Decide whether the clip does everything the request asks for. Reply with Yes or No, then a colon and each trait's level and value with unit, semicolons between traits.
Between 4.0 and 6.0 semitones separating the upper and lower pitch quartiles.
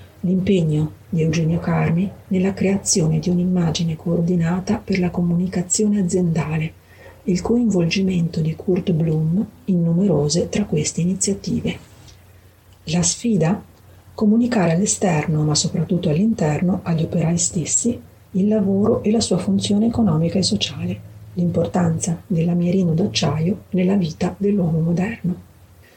No: average, 3.2 semitones